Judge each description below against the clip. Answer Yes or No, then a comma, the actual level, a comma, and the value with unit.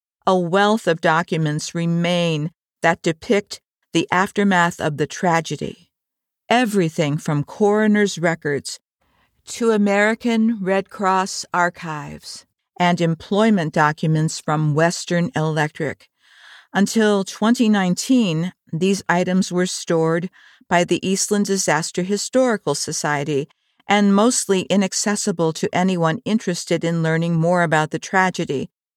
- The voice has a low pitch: No, medium, 180 Hz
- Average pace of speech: No, slow, 105 wpm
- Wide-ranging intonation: No, average, 3.8 semitones